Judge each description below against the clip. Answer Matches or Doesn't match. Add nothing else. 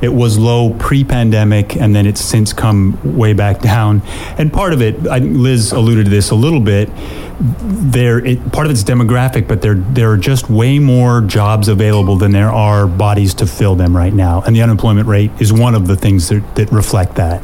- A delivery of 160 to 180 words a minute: Doesn't match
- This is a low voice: Matches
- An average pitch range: Matches